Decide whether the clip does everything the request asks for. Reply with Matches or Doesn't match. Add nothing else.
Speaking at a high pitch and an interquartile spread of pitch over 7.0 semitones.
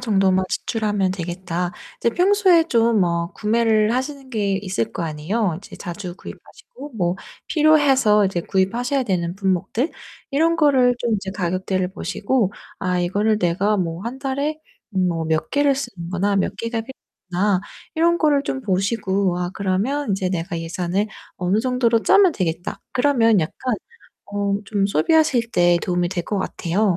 Doesn't match